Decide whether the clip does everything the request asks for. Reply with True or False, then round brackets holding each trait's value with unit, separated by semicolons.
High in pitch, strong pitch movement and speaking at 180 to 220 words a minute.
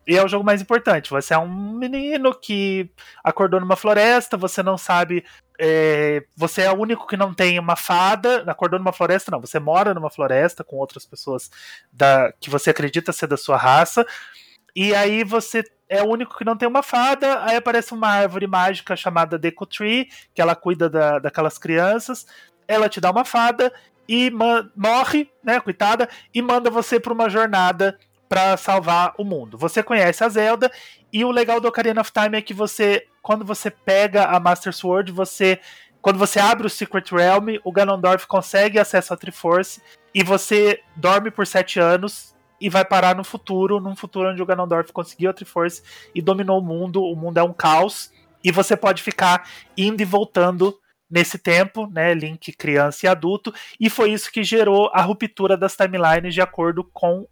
False (195 Hz; 3.6 semitones; 185 wpm)